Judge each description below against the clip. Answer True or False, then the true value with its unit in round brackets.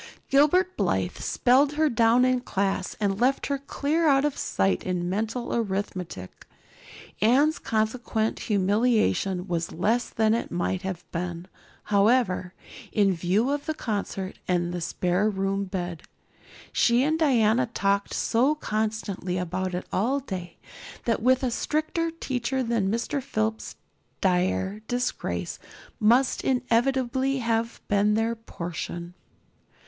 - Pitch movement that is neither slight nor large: True (5.0 semitones)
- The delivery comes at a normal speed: False (130 wpm)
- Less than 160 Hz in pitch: False (220 Hz)